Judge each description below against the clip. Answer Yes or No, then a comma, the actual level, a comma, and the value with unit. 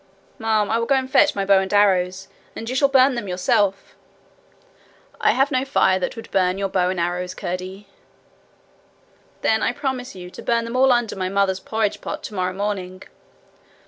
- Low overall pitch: No, high, 200 Hz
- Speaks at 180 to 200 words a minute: Yes, average, 185 wpm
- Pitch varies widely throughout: No, average, 4.2 semitones